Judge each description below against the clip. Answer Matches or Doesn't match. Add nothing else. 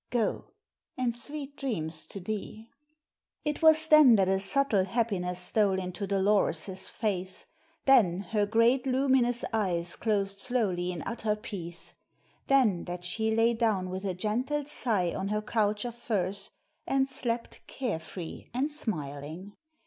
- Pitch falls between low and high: Doesn't match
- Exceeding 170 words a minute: Doesn't match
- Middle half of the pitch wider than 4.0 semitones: Matches